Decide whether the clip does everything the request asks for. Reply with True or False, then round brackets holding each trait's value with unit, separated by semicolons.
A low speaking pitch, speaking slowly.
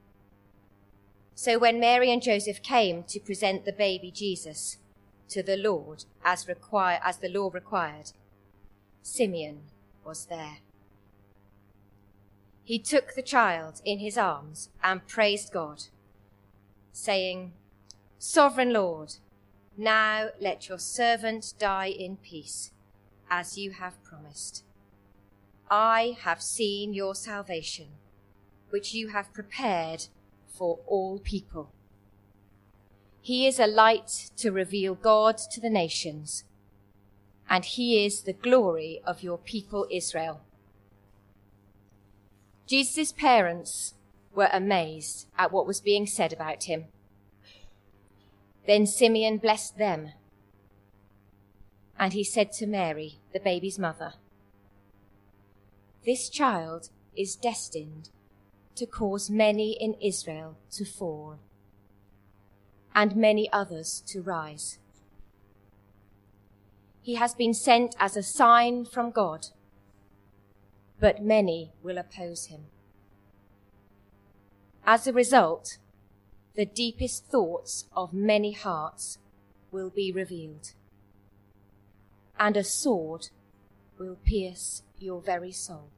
False (160 Hz; 105 wpm)